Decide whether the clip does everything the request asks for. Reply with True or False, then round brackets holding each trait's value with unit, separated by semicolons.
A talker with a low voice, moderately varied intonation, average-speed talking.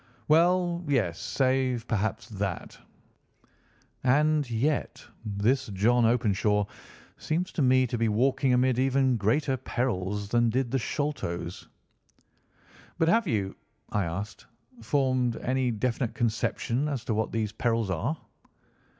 False (120 Hz; 3.7 semitones; 125 wpm)